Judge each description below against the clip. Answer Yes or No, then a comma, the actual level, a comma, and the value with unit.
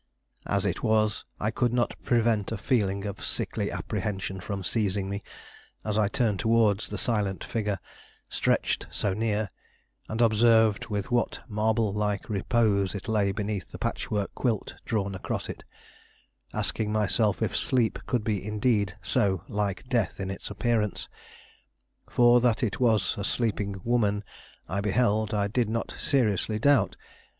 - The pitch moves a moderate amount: No, narrow, 2.3 semitones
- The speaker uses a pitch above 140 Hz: No, low, 105 Hz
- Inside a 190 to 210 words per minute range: No, average, 150 wpm